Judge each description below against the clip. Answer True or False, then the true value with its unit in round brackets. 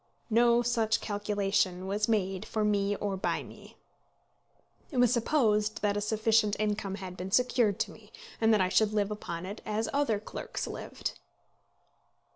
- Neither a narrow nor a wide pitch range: False (2.1 semitones)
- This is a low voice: False (210 Hz)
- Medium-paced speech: True (160 wpm)